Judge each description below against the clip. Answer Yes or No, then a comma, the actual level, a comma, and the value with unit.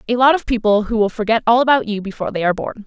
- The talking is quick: Yes, fast, 295 wpm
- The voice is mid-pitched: No, high, 225 Hz